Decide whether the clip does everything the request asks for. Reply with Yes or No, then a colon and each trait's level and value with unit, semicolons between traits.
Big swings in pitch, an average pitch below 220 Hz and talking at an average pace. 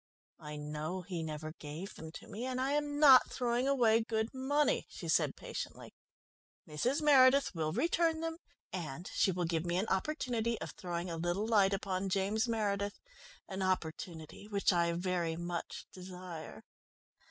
Yes: wide, 6.1 semitones; high, 190 Hz; average, 160 wpm